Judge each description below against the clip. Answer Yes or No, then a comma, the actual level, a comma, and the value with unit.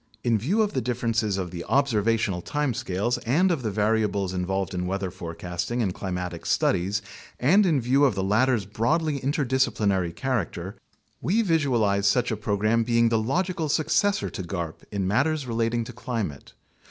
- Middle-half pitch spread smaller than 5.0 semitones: No, wide, 5.4 semitones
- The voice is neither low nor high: No, low, 115 Hz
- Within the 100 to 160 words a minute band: No, average, 170 wpm